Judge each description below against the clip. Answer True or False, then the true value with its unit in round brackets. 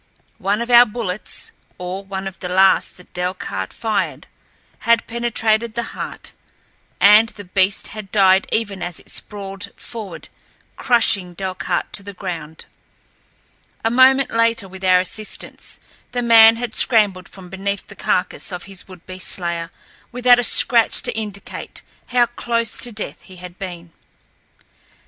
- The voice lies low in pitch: False (200 Hz)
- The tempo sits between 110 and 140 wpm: False (150 wpm)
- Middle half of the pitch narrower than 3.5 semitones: False (3.8 semitones)